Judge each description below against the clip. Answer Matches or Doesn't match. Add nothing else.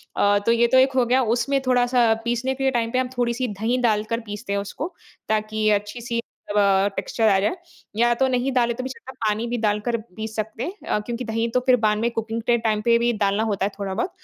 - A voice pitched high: Matches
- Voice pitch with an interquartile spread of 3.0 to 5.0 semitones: Doesn't match